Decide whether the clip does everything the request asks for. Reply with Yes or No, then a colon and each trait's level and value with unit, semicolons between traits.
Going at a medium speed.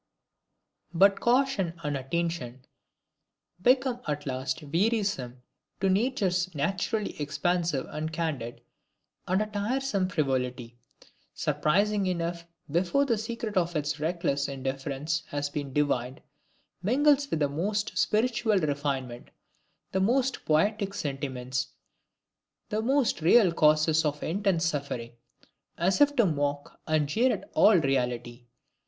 No: slow, 115 wpm